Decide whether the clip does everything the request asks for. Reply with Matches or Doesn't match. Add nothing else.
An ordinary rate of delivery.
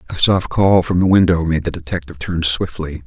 Doesn't match